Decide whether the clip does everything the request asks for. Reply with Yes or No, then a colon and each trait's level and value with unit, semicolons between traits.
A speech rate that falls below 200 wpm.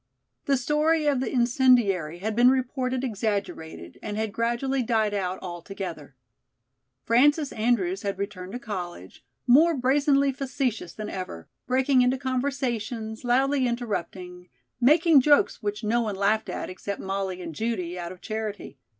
Yes: average, 140 wpm